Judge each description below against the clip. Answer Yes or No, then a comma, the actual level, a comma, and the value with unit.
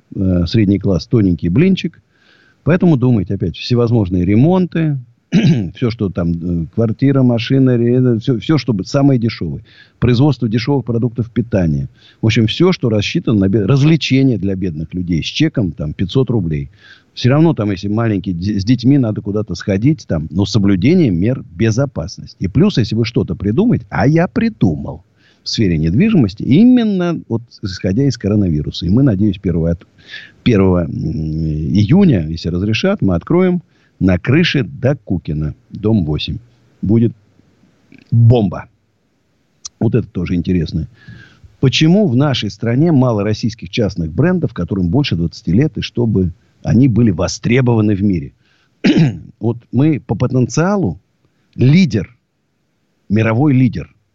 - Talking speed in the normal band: Yes, average, 135 wpm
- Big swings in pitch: Yes, wide, 6.2 semitones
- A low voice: Yes, low, 115 Hz